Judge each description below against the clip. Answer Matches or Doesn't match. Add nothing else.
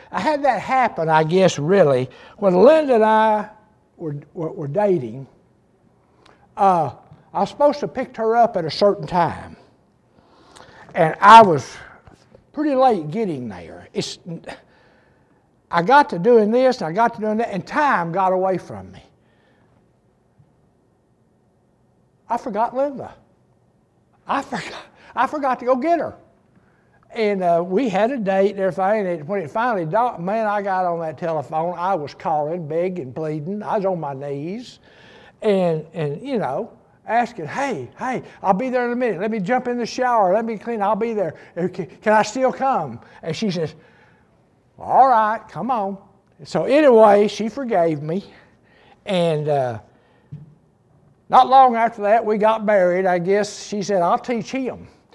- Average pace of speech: Matches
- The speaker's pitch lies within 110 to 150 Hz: Doesn't match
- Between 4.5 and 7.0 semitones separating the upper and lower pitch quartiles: Matches